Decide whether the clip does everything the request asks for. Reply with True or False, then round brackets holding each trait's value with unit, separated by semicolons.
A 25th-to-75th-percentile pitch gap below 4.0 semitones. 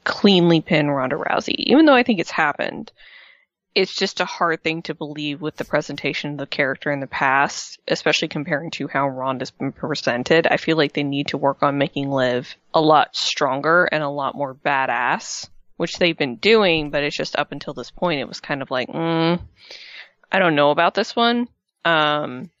True (3.2 semitones)